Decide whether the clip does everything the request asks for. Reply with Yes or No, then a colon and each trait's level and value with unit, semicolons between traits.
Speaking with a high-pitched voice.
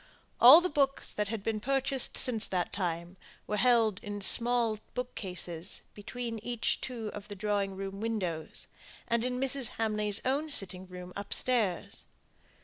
Yes: high, 215 Hz